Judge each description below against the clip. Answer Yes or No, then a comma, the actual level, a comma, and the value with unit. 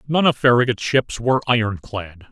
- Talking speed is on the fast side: No, average, 155 wpm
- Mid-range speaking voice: No, low, 120 Hz